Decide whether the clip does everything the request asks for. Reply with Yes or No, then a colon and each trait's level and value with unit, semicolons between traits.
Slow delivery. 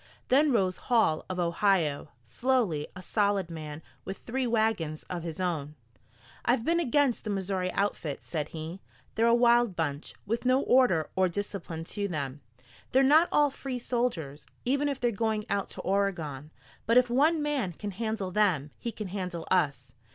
No: average, 170 wpm